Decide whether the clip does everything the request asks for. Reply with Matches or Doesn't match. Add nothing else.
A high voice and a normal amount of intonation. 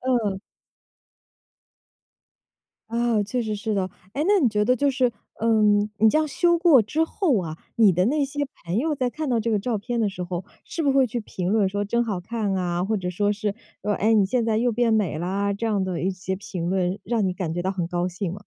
Matches